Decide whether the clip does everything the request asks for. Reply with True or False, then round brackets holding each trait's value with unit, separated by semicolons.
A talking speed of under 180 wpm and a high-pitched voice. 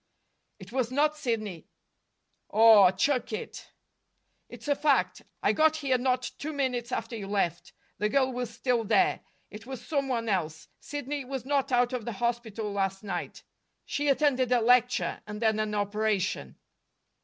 True (160 wpm; 240 Hz)